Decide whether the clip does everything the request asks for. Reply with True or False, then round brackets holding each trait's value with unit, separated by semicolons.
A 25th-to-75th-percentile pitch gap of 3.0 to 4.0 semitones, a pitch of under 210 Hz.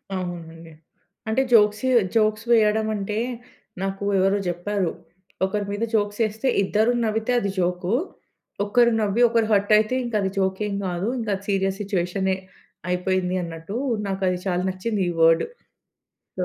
False (2.6 semitones; 200 Hz)